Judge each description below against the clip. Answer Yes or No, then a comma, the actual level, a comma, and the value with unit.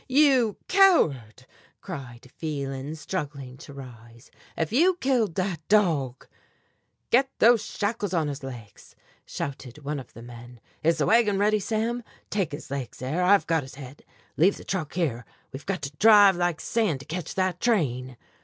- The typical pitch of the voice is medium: Yes, medium, 160 Hz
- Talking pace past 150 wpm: Yes, average, 165 wpm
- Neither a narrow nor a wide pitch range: No, wide, 7.4 semitones